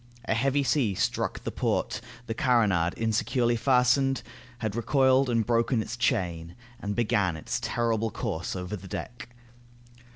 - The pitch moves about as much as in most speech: Yes, average, 3.6 semitones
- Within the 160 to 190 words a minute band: No, average, 140 wpm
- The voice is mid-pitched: No, low, 115 Hz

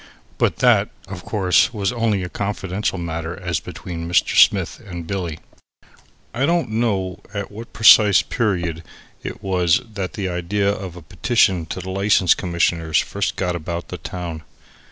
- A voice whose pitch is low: Yes, very low, 95 Hz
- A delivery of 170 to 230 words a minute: No, average, 155 wpm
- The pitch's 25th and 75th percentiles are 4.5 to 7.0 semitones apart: No, average, 3.0 semitones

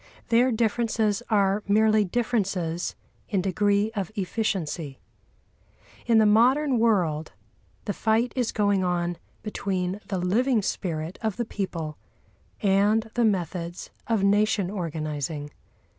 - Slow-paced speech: Yes, slow, 115 wpm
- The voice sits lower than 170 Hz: No, high, 200 Hz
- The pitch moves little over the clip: No, average, 3.7 semitones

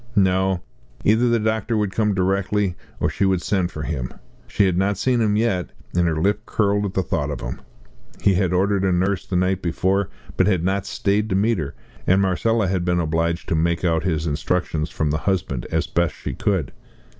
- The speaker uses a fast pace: Yes, fast, 210 wpm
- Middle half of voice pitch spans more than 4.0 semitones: No, average, 2.8 semitones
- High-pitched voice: No, very low, 95 Hz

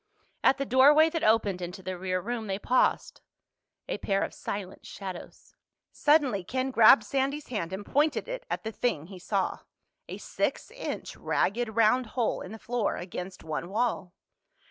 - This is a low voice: No, high, 220 Hz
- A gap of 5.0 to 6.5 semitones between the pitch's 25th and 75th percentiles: Yes, average, 5.3 semitones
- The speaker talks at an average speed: Yes, average, 165 wpm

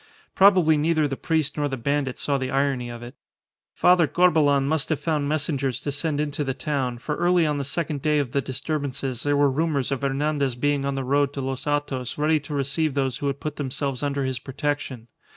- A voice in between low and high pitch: Yes, medium, 145 Hz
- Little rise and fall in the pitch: Yes, narrow, 2.0 semitones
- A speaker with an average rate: No, fast, 215 wpm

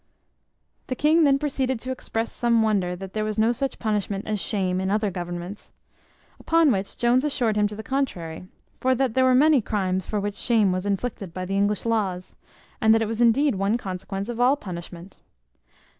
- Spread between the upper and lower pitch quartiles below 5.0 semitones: Yes, average, 4.4 semitones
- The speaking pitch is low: No, high, 215 Hz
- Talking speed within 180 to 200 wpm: Yes, average, 195 wpm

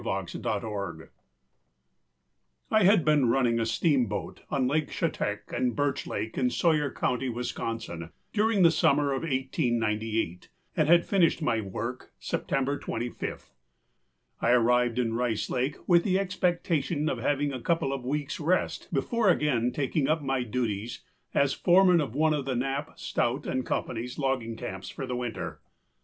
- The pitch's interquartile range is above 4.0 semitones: Yes, average, 4.6 semitones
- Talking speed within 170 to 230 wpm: No, average, 145 wpm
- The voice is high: No, low, 135 Hz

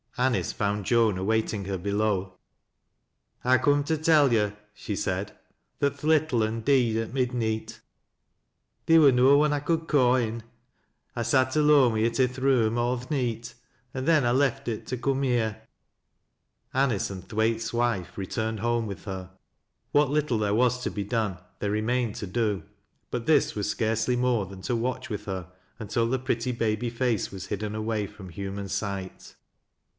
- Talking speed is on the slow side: No, average, 180 wpm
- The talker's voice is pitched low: Yes, low, 115 Hz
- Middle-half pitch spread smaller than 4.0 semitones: Yes, average, 3.5 semitones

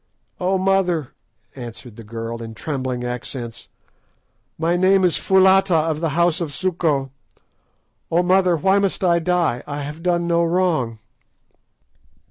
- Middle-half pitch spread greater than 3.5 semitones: Yes, wide, 5.5 semitones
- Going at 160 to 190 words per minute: No, slow, 135 wpm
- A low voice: No, medium, 165 Hz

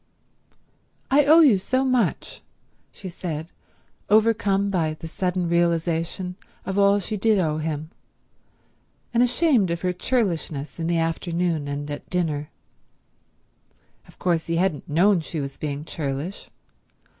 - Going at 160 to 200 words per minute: No, slow, 135 wpm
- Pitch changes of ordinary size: Yes, average, 4.0 semitones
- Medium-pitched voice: Yes, medium, 175 Hz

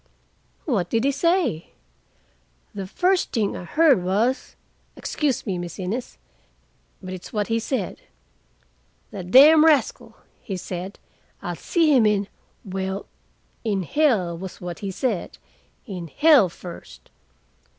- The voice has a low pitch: No, high, 205 Hz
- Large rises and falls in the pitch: Yes, wide, 6.7 semitones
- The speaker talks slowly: Yes, slow, 120 wpm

